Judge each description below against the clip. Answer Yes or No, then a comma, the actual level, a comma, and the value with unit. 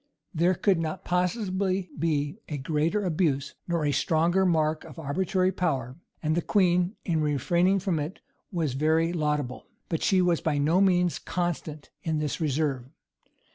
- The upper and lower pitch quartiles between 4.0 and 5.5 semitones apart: No, average, 3.2 semitones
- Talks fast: No, average, 160 wpm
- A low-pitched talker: No, medium, 165 Hz